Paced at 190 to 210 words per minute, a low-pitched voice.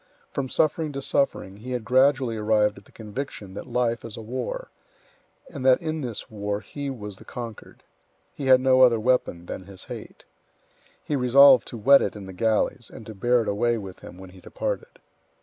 Yes: average, 200 wpm; low, 120 Hz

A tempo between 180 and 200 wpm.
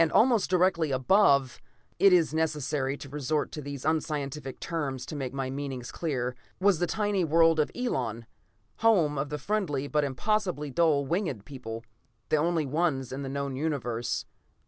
No: average, 155 wpm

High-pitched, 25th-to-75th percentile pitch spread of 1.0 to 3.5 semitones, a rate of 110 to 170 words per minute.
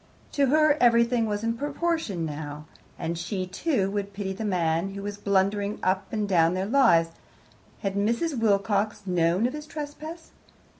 No: high, 205 Hz; average, 4.5 semitones; average, 160 wpm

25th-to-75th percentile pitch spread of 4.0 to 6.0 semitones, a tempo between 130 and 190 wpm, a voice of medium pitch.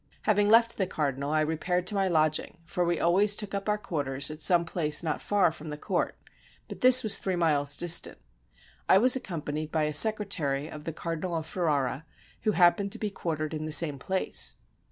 No: average, 4.3 semitones; average, 200 wpm; medium, 170 Hz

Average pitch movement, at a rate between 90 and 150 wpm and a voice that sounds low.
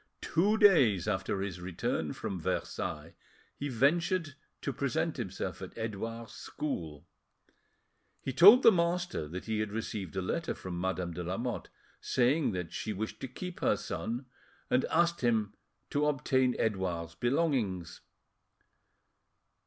No: wide, 8.0 semitones; slow, 135 wpm; low, 115 Hz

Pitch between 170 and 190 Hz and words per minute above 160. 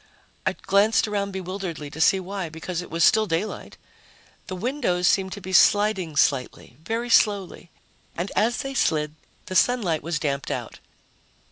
No: medium, 185 Hz; average, 155 wpm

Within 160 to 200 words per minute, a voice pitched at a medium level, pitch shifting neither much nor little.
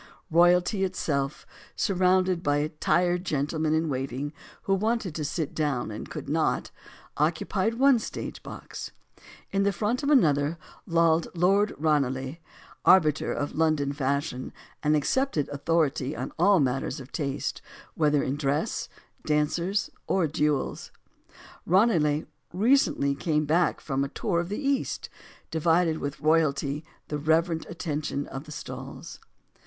No: slow, 135 wpm; medium, 160 Hz; average, 3.9 semitones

